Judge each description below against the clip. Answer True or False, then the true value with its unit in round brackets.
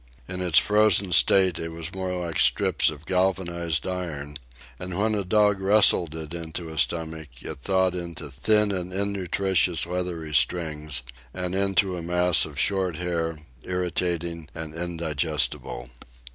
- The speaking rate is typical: True (145 wpm)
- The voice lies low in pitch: True (85 Hz)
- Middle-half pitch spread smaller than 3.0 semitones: True (2.6 semitones)